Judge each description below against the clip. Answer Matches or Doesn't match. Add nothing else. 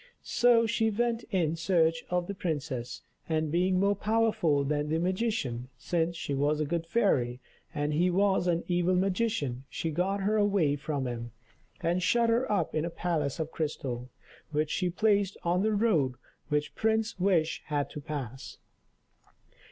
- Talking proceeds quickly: Doesn't match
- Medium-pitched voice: Matches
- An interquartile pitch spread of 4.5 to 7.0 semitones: Matches